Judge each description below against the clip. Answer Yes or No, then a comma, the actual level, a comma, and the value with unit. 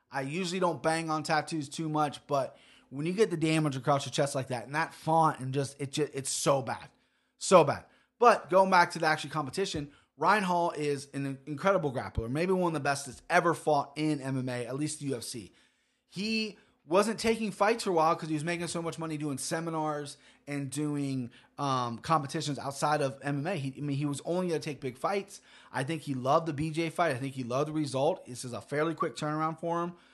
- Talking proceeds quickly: Yes, fast, 225 wpm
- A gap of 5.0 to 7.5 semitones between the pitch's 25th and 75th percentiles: No, average, 3.2 semitones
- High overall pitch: No, medium, 150 Hz